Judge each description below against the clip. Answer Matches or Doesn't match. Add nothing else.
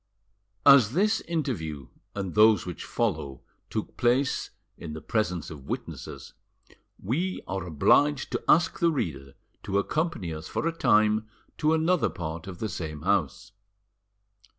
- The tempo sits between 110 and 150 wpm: Matches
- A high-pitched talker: Doesn't match